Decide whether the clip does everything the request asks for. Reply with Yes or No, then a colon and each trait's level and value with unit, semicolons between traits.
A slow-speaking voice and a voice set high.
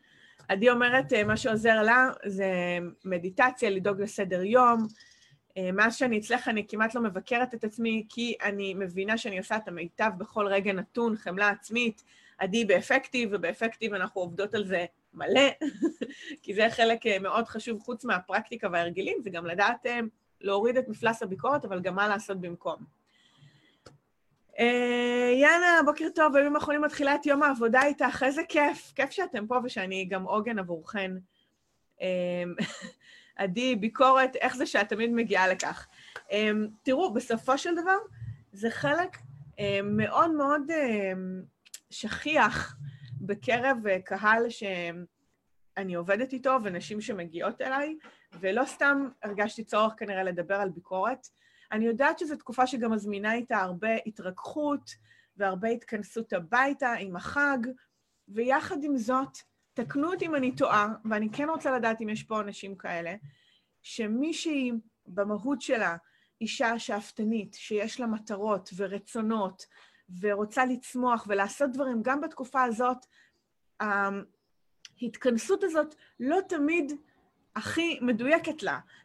Yes: slow, 130 wpm; high, 225 Hz